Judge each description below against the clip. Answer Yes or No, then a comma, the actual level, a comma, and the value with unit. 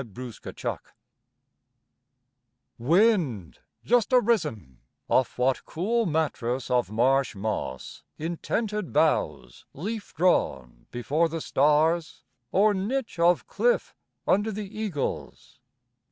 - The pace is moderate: No, slow, 100 wpm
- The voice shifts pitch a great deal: Yes, wide, 9.0 semitones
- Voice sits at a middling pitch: Yes, medium, 160 Hz